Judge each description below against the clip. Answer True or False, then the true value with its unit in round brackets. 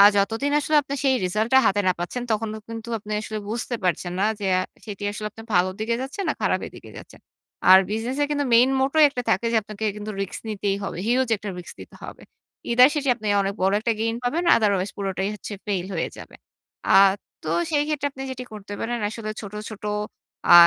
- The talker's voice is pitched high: True (215 Hz)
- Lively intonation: False (3.8 semitones)